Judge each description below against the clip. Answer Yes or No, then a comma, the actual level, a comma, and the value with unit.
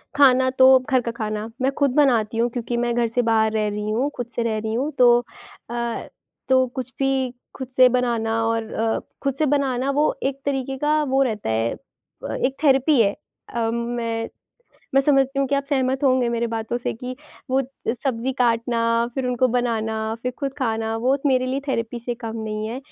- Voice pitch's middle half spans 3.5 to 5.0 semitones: No, average, 2.8 semitones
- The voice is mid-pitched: No, high, 245 Hz